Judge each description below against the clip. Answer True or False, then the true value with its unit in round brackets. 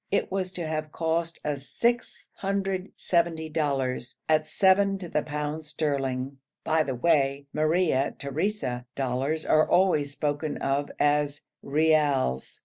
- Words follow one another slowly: True (125 wpm)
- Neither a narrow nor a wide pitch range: True (3.3 semitones)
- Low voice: False (155 Hz)